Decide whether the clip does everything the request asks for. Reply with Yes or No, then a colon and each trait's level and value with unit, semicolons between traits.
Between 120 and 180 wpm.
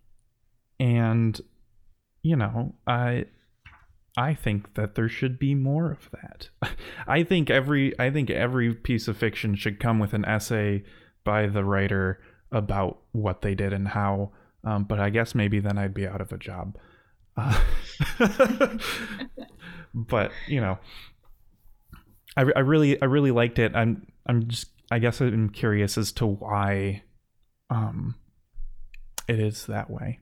Yes: average, 145 wpm